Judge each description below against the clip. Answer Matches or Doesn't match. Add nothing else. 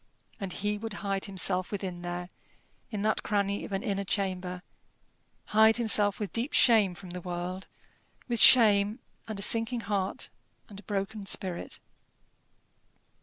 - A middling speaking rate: Matches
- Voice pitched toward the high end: Matches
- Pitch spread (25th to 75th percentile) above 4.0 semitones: Doesn't match